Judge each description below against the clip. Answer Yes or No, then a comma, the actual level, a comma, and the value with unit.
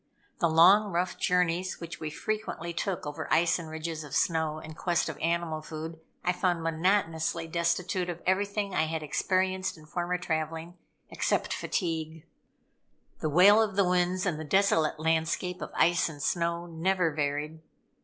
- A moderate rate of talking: Yes, average, 160 wpm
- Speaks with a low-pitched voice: No, medium, 170 Hz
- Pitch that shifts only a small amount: Yes, narrow, 2.3 semitones